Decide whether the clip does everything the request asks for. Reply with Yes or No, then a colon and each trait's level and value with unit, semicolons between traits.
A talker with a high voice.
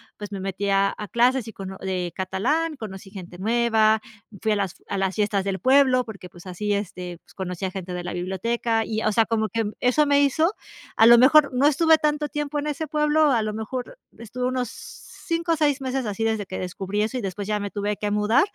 Yes: high, 220 Hz